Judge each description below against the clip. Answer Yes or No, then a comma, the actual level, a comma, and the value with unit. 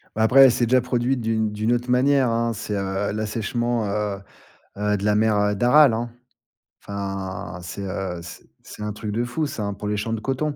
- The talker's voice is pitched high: No, low, 110 Hz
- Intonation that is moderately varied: Yes, average, 3.0 semitones